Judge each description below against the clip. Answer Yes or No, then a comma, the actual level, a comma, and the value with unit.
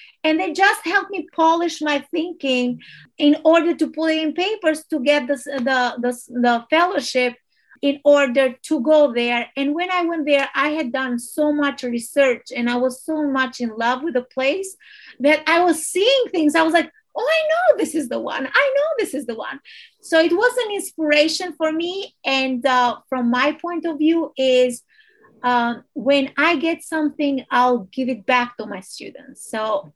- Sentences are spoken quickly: No, average, 190 wpm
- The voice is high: Yes, very high, 295 Hz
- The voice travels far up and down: No, average, 4.4 semitones